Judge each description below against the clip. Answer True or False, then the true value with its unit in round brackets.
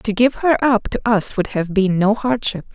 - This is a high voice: True (220 Hz)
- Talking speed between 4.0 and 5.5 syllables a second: True (4.5 syllables/s)